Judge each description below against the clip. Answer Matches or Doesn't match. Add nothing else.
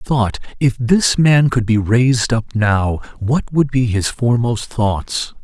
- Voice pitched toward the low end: Matches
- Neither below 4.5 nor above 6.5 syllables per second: Doesn't match